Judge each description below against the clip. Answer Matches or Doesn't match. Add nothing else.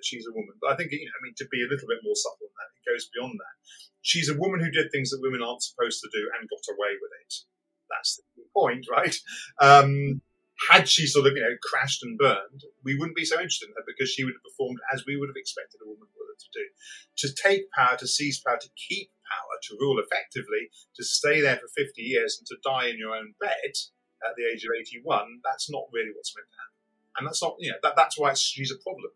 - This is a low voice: Doesn't match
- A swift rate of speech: Matches